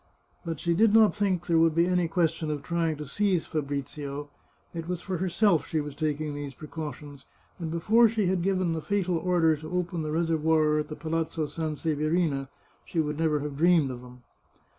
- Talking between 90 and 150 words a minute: No, average, 200 wpm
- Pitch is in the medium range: Yes, medium, 160 Hz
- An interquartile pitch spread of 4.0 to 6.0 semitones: No, average, 2.8 semitones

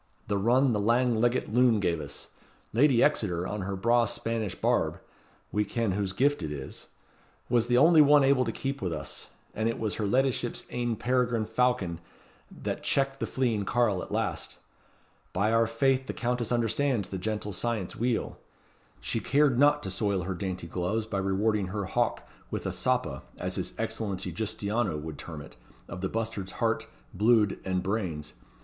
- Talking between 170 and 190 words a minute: Yes, average, 175 wpm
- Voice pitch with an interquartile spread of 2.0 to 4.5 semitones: Yes, average, 4.2 semitones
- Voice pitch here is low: Yes, low, 110 Hz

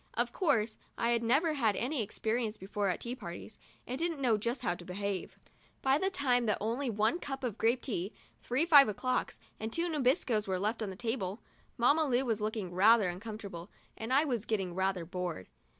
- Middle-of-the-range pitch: No, high, 225 Hz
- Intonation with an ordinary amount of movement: Yes, average, 4.4 semitones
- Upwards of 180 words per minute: Yes, average, 200 wpm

